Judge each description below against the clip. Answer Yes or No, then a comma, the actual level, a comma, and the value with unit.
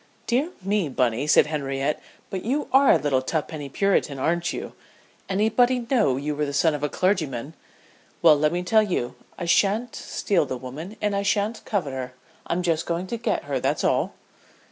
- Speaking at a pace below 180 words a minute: No, average, 190 wpm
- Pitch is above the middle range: No, medium, 170 Hz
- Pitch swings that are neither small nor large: No, wide, 6.3 semitones